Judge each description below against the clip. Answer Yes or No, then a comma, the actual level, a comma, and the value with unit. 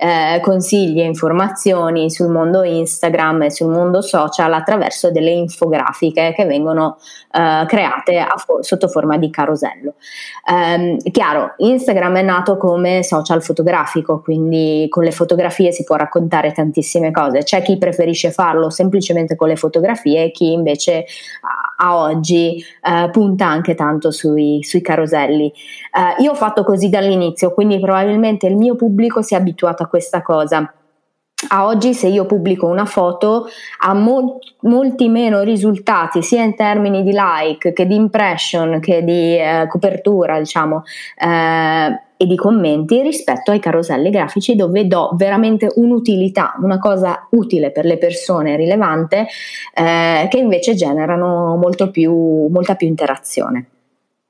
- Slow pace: No, average, 145 wpm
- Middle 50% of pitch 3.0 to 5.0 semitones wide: Yes, average, 3.7 semitones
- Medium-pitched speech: Yes, medium, 175 Hz